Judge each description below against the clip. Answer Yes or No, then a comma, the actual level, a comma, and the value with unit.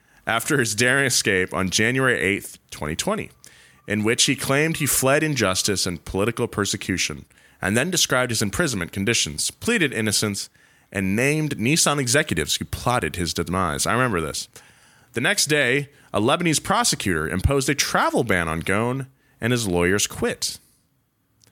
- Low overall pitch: Yes, low, 115 Hz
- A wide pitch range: Yes, wide, 6.6 semitones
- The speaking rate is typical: Yes, average, 150 wpm